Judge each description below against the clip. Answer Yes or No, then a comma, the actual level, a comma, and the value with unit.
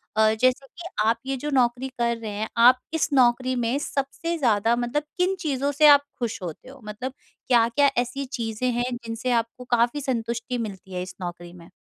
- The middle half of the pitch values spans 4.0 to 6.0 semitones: No, average, 2.9 semitones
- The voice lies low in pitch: No, high, 245 Hz